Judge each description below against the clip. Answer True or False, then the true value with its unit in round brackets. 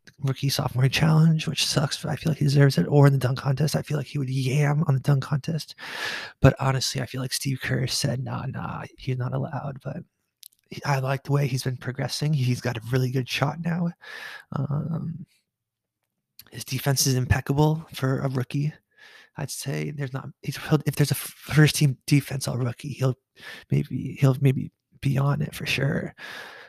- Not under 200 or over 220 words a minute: False (190 wpm)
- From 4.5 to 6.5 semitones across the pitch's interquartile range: False (2.7 semitones)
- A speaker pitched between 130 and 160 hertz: True (140 Hz)